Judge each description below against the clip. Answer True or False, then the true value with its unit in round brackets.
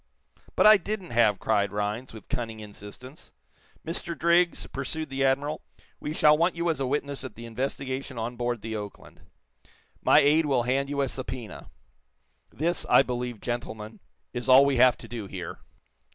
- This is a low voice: True (130 Hz)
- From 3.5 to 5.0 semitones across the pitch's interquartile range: True (4.1 semitones)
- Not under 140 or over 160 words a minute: False (170 wpm)